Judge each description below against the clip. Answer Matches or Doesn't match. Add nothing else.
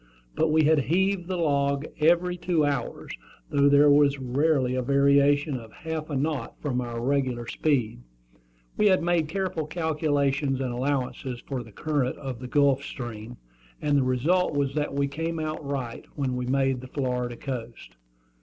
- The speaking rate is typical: Matches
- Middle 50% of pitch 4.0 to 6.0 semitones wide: Doesn't match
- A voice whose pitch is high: Doesn't match